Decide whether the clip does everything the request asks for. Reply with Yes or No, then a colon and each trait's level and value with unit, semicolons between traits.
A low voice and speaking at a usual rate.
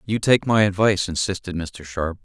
Yes: very low, 95 Hz; average, 190 wpm